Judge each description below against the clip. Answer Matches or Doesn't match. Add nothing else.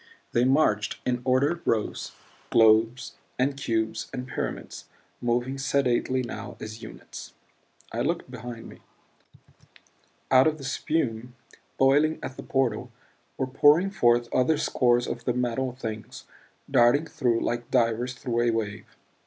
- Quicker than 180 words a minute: Doesn't match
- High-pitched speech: Doesn't match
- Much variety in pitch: Doesn't match